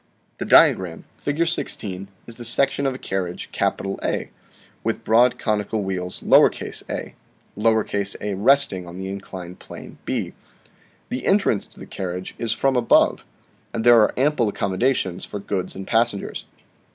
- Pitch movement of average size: Yes, average, 4.2 semitones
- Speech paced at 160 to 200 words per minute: No, average, 140 wpm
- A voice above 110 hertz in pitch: No, low, 105 Hz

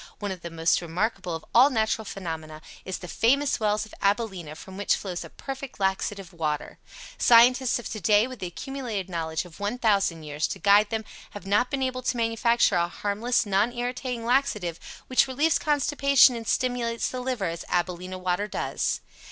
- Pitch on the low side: No, high, 210 Hz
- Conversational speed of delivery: Yes, average, 175 wpm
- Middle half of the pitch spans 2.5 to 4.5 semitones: No, wide, 5.4 semitones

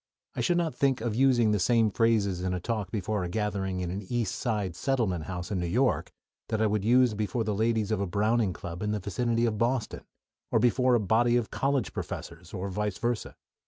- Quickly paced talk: Yes, fast, 220 wpm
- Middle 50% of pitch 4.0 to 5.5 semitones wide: No, average, 3.6 semitones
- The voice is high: No, low, 110 Hz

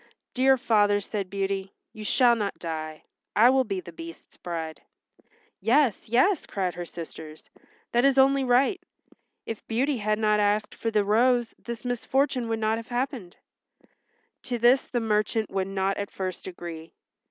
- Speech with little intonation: No, average, 4.3 semitones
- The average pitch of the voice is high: Yes, high, 215 Hz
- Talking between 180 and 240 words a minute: No, average, 160 wpm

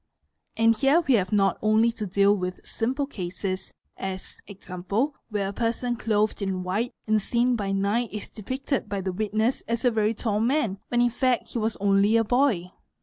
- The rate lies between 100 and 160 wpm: No, average, 190 wpm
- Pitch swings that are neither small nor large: Yes, average, 3.2 semitones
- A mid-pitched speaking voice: No, high, 215 Hz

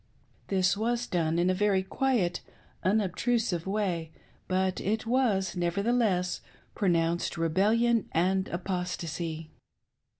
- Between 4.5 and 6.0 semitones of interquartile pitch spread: No, average, 3.8 semitones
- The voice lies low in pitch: No, high, 190 Hz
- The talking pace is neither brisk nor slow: No, slow, 100 wpm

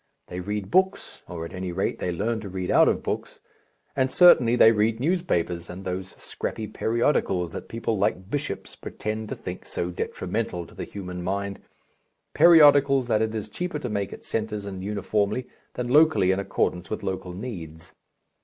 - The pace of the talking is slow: No, average, 175 wpm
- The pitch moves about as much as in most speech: Yes, average, 4.7 semitones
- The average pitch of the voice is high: No, low, 105 Hz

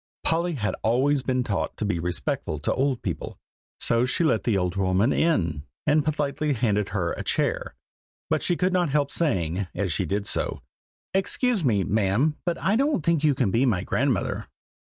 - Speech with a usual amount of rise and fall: No, wide, 7.9 semitones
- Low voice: Yes, low, 125 Hz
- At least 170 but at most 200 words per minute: Yes, average, 185 wpm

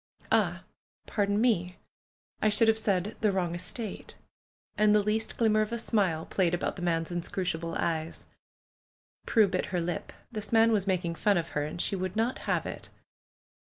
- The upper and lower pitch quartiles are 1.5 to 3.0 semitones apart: No, average, 3.7 semitones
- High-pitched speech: Yes, high, 195 Hz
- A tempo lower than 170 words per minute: No, average, 180 wpm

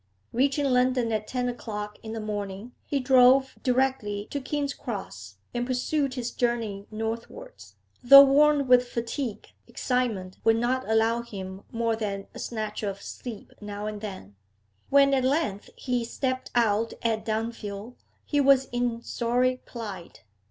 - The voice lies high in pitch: Yes, high, 235 Hz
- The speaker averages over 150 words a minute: No, average, 145 wpm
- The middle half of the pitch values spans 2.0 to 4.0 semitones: Yes, average, 3.3 semitones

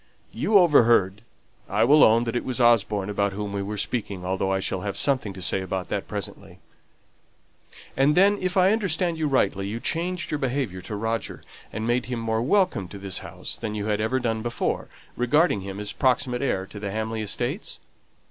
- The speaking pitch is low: Yes, low, 110 Hz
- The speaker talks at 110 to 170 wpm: No, average, 195 wpm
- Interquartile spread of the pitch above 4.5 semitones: Yes, average, 5.2 semitones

